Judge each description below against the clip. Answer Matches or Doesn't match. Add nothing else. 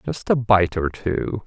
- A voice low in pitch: Matches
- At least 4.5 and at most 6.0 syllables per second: Doesn't match